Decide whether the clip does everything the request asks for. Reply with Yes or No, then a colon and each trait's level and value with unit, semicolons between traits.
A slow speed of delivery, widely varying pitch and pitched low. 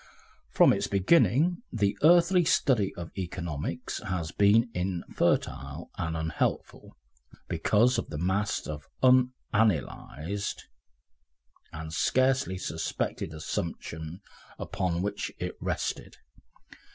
Yes: slow, 95 wpm; wide, 6.6 semitones; very low, 95 Hz